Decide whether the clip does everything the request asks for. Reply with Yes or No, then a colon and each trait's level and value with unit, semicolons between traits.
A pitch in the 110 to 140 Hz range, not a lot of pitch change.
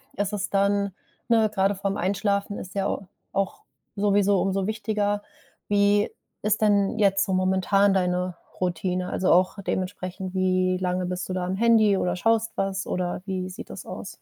No: high, 195 Hz; narrow, 1.7 semitones